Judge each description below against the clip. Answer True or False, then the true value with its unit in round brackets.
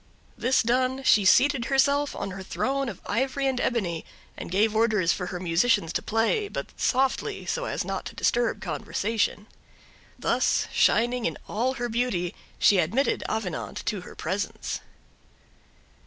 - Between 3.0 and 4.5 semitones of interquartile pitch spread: False (5.3 semitones)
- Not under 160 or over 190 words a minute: False (150 wpm)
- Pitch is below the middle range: False (230 Hz)